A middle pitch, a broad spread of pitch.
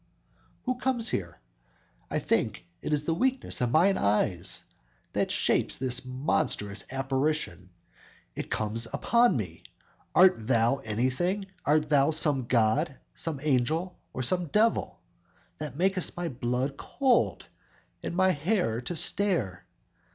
Yes: medium, 145 Hz; wide, 6.7 semitones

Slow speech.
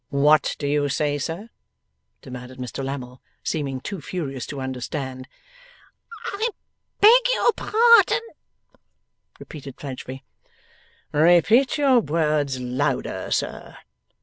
Yes: slow, 100 wpm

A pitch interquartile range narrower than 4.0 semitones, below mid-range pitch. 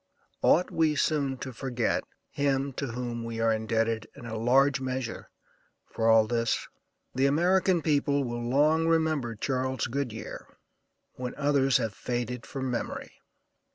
Yes: average, 3.4 semitones; low, 130 Hz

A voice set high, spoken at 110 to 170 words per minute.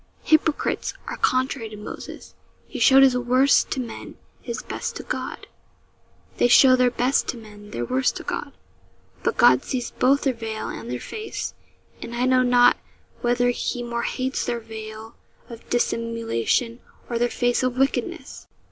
Yes: high, 240 Hz; average, 165 wpm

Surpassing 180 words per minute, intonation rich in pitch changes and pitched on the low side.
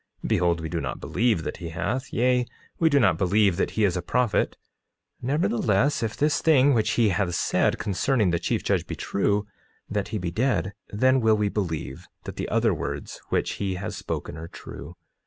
Yes: average, 195 wpm; wide, 5.8 semitones; low, 105 Hz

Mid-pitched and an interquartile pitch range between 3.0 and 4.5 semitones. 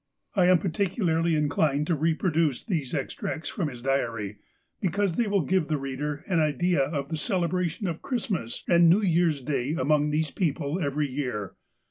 Yes: medium, 160 Hz; average, 4.0 semitones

